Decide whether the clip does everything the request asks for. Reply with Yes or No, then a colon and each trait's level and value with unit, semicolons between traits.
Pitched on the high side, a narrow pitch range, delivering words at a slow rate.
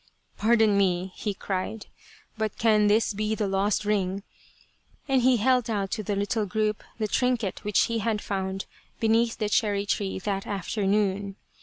No: high, 210 Hz; narrow, 2.1 semitones; average, 175 wpm